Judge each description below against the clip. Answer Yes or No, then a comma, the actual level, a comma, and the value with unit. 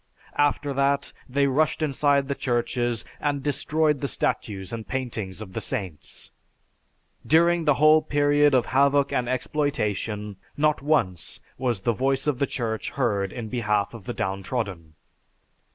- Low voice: Yes, low, 130 Hz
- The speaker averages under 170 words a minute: Yes, average, 145 wpm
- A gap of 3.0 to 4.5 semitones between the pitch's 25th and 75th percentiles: No, average, 5.2 semitones